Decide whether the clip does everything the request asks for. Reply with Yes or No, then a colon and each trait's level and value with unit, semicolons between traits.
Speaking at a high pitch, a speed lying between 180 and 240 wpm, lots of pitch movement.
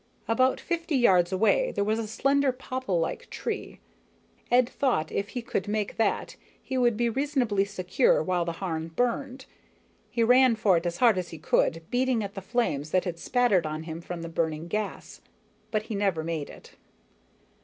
Yes: high, 210 Hz; average, 185 wpm; wide, 6.3 semitones